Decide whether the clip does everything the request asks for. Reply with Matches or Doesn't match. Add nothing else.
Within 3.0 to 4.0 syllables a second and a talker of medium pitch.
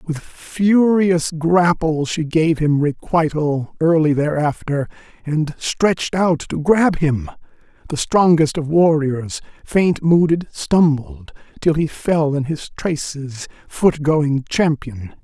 Matches